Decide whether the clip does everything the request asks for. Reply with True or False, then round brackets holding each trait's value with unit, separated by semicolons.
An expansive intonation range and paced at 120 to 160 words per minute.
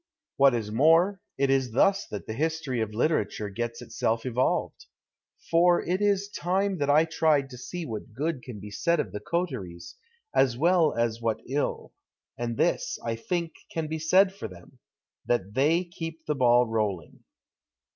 False (6.5 semitones; 175 wpm)